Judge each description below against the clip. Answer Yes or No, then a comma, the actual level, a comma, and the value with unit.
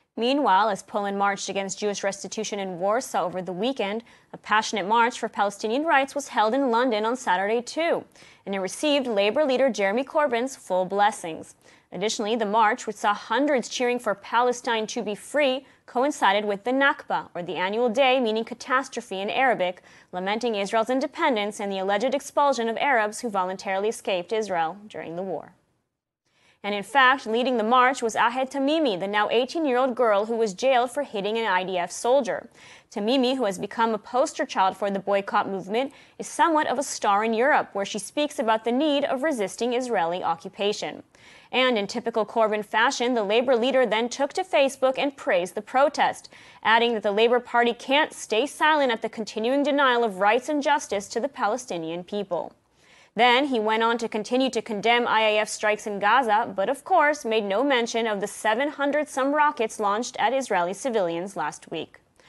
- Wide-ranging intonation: No, average, 4.3 semitones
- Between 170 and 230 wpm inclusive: Yes, average, 180 wpm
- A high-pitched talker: Yes, high, 230 Hz